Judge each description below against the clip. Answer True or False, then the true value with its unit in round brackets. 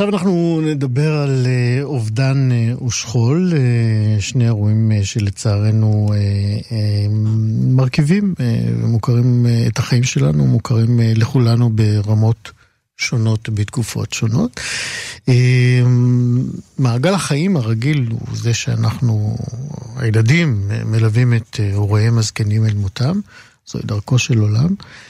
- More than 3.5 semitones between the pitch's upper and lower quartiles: False (2.9 semitones)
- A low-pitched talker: True (115 Hz)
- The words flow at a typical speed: False (90 wpm)